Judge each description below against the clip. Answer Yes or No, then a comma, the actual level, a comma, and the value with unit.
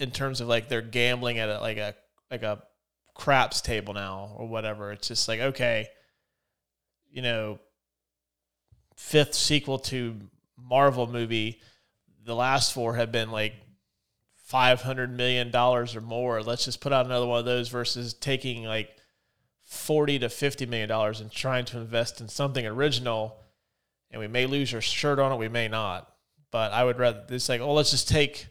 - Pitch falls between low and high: No, low, 120 Hz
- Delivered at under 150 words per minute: No, average, 175 wpm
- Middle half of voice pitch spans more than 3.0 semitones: No, average, 2.7 semitones